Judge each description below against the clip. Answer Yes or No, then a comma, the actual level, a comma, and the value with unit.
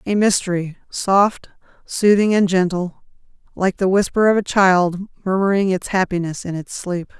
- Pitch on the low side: No, high, 190 Hz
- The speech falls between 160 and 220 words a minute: No, average, 150 wpm